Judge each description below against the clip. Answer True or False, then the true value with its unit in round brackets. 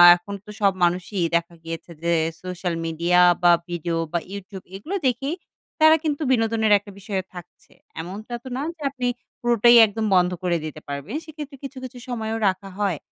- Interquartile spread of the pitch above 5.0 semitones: True (5.5 semitones)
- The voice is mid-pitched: False (200 Hz)